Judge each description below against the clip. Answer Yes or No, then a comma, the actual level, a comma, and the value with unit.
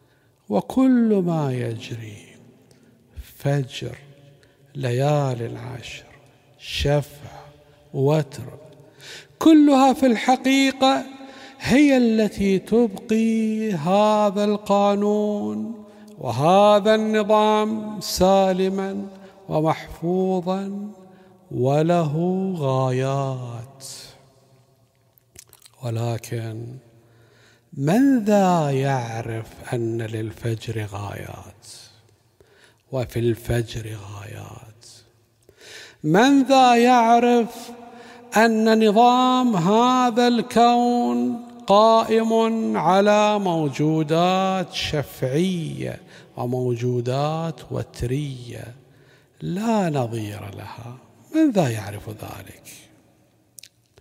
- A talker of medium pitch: Yes, medium, 155 Hz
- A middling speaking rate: No, slow, 60 wpm